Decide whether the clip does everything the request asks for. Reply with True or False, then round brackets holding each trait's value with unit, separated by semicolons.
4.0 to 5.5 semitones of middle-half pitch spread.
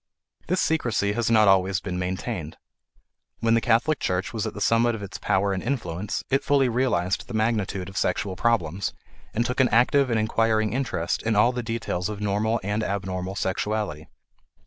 False (3.5 semitones)